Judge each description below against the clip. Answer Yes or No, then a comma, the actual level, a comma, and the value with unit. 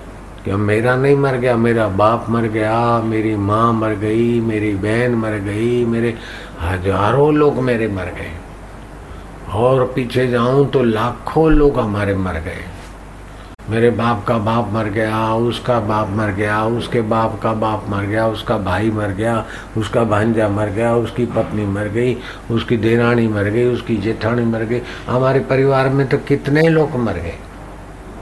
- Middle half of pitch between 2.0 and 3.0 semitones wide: Yes, narrow, 2.4 semitones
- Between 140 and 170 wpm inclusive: Yes, average, 160 wpm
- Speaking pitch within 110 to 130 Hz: Yes, low, 115 Hz